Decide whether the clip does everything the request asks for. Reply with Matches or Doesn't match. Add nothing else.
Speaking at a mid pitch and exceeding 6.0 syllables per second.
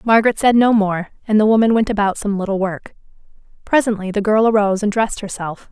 Doesn't match